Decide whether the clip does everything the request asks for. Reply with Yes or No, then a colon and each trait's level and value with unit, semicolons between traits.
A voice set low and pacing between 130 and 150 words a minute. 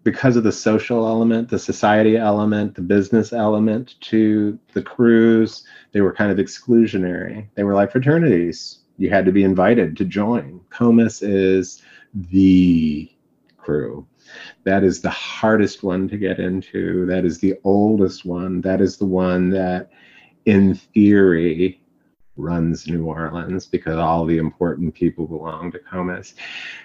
Yes: very low, 95 Hz; average, 145 wpm